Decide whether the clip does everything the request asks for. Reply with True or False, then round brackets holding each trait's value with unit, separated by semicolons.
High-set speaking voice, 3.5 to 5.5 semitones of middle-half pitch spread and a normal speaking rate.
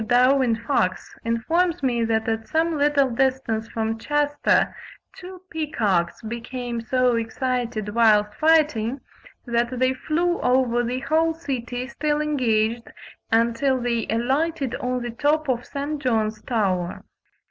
False (250 Hz; 4.1 semitones; 125 wpm)